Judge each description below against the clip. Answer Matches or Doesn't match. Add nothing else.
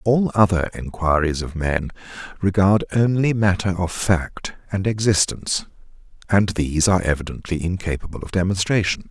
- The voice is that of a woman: Doesn't match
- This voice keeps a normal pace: Doesn't match